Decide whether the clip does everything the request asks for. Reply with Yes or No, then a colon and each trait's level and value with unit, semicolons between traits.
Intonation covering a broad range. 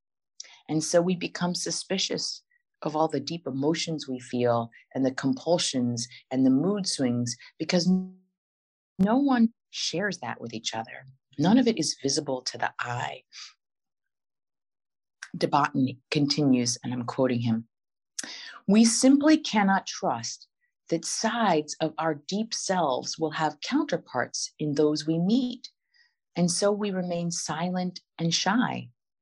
Yes: wide, 6.9 semitones